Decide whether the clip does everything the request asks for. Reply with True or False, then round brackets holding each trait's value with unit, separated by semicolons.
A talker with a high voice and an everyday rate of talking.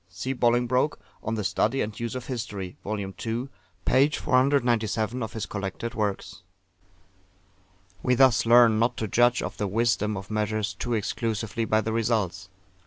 False (115 Hz; 155 wpm)